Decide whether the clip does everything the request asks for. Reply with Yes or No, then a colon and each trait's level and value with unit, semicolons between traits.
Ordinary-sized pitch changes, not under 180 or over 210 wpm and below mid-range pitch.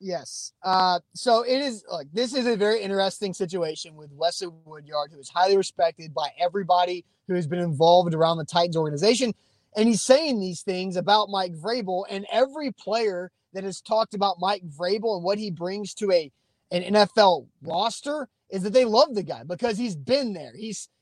No: average, 4.0 semitones; average, 190 wpm; high, 190 Hz